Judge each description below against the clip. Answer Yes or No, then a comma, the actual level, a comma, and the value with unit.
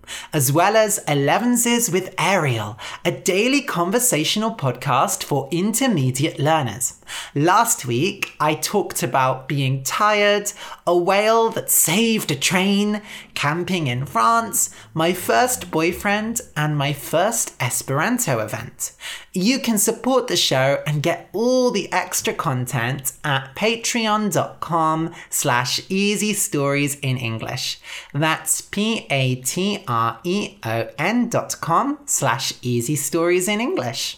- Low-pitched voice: No, medium, 170 Hz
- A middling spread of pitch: No, wide, 7.1 semitones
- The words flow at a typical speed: No, slow, 110 wpm